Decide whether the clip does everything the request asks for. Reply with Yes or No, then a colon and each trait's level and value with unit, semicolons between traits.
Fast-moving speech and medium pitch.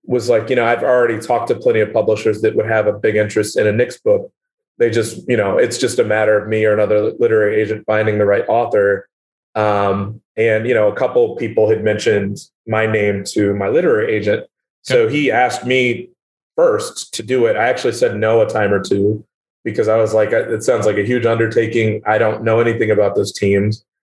No: fast, 220 wpm; low, 120 Hz